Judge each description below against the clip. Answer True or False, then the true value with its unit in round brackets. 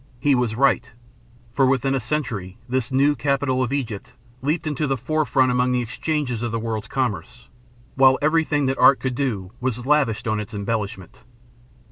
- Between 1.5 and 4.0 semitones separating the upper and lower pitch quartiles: True (3.2 semitones)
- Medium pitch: False (130 Hz)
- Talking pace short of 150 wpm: False (170 wpm)